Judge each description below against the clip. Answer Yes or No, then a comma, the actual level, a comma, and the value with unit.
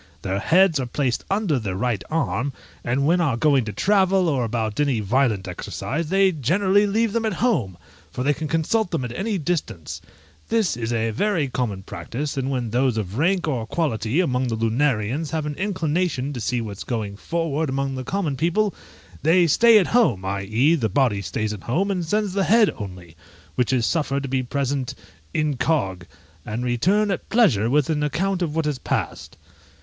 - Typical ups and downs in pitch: No, wide, 7.2 semitones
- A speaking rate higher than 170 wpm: Yes, average, 190 wpm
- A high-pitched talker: No, medium, 140 Hz